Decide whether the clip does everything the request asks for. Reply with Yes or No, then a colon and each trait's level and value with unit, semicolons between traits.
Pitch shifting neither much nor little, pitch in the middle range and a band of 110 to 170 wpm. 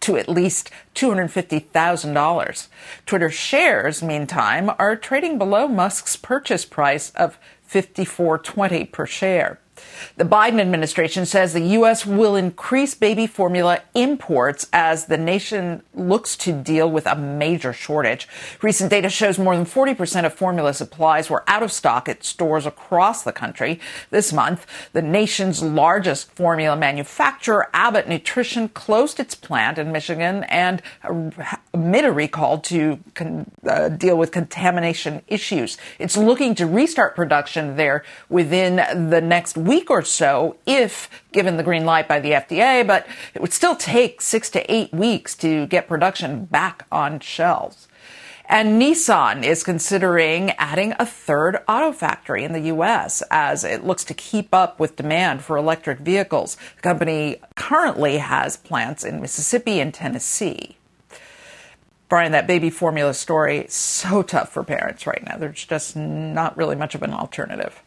Yes: average, 4.5 semitones; medium, 175 Hz; average, 150 wpm